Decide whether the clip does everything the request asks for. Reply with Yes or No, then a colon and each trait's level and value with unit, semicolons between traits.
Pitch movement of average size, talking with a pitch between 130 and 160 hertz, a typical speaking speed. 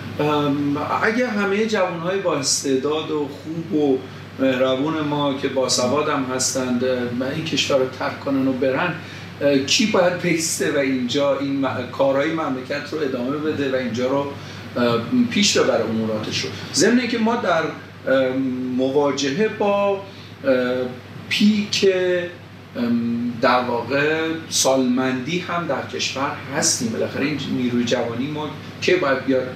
Yes: average, 3.8 semitones; medium, 140 Hz; average, 130 wpm